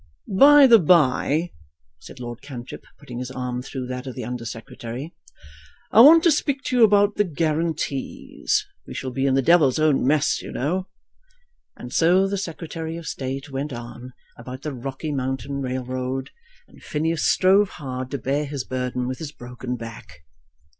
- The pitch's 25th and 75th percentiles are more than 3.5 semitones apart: Yes, average, 4.9 semitones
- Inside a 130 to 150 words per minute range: No, average, 175 wpm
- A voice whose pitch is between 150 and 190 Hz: No, medium, 140 Hz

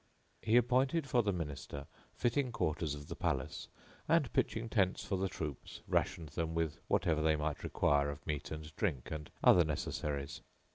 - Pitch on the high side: No, very low, 80 Hz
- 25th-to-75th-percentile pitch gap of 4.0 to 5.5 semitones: Yes, average, 5.1 semitones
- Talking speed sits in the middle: Yes, average, 170 wpm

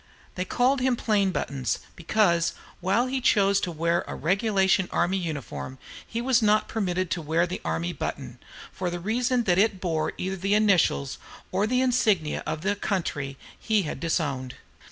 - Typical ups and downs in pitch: Yes, average, 4.4 semitones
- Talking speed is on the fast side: No, average, 175 wpm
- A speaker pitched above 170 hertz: Yes, high, 190 Hz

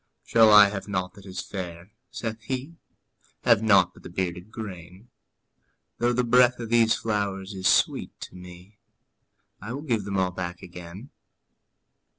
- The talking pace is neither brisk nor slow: Yes, average, 160 wpm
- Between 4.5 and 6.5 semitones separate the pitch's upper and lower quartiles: No, average, 3.7 semitones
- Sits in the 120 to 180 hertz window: No, low, 100 Hz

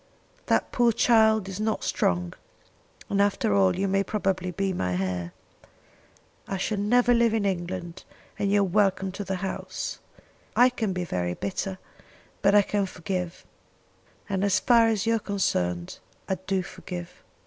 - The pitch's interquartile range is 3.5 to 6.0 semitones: No, narrow, 2.6 semitones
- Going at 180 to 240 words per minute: No, average, 160 wpm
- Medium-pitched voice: No, high, 195 Hz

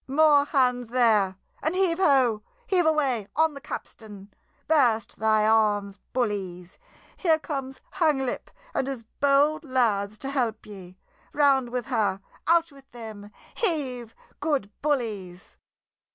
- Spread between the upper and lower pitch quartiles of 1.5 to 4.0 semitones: No, average, 5.3 semitones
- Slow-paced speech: Yes, slow, 125 wpm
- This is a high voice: Yes, very high, 250 Hz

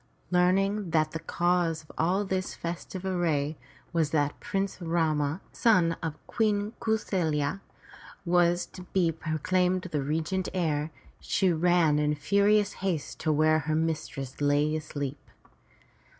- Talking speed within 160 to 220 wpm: No, slow, 135 wpm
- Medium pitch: Yes, medium, 165 Hz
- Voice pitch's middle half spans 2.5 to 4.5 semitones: Yes, average, 3.3 semitones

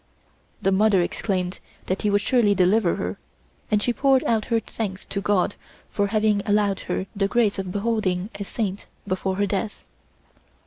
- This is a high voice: Yes, high, 205 Hz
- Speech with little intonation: Yes, narrow, 2.2 semitones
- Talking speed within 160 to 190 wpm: Yes, average, 170 wpm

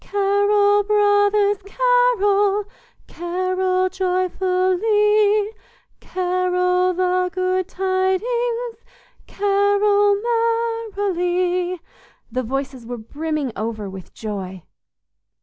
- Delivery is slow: Yes, slow, 70 wpm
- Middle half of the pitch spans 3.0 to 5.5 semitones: No, narrow, 2.4 semitones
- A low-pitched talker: No, very high, 375 Hz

